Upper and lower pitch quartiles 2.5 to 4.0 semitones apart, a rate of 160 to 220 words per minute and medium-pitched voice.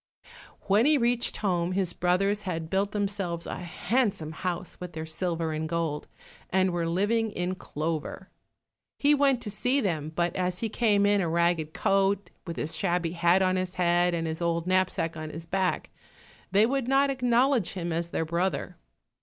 Yes: average, 3.3 semitones; average, 180 wpm; medium, 180 Hz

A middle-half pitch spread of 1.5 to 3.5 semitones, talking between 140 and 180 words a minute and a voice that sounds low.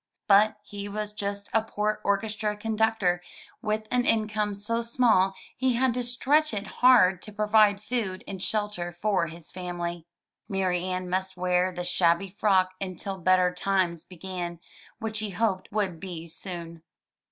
No: average, 3.0 semitones; average, 150 wpm; high, 200 Hz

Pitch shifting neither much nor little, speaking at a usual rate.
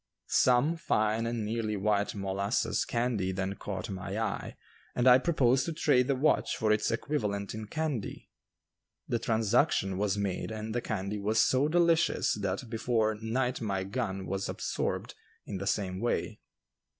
Yes: average, 3.8 semitones; average, 155 wpm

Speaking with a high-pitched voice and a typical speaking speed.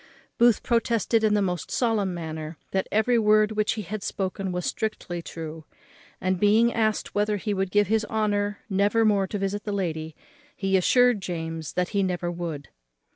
Yes: high, 200 Hz; average, 180 wpm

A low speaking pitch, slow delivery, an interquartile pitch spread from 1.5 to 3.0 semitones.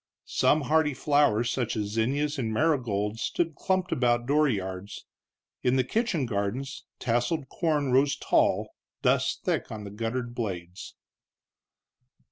No: low, 125 Hz; slow, 125 wpm; average, 5.0 semitones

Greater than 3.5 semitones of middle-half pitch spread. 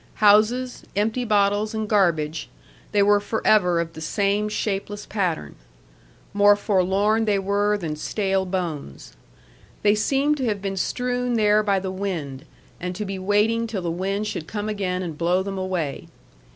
No: narrow, 2.6 semitones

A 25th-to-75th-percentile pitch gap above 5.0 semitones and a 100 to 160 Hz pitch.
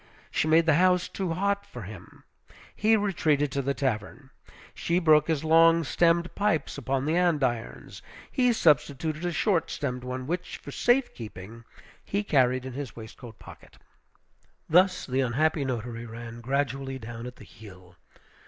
Yes: wide, 5.5 semitones; medium, 140 Hz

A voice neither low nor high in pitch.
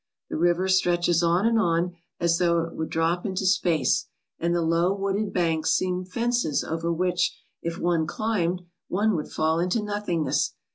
Yes: medium, 175 Hz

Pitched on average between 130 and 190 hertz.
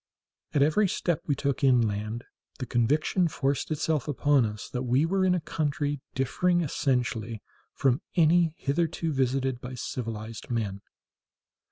Yes: low, 135 Hz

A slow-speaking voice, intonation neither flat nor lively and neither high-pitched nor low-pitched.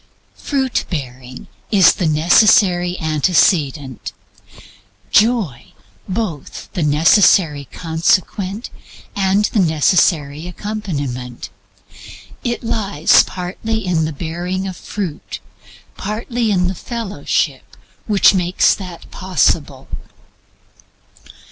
Yes: slow, 85 wpm; average, 4.8 semitones; medium, 180 Hz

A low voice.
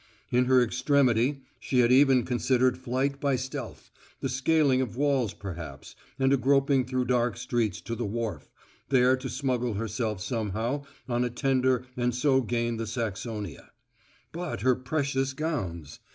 Yes: low, 125 Hz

